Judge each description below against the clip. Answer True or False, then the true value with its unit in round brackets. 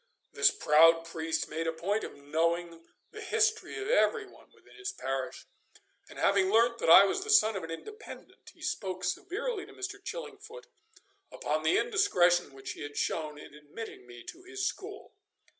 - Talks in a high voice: True (195 Hz)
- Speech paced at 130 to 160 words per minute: False (175 wpm)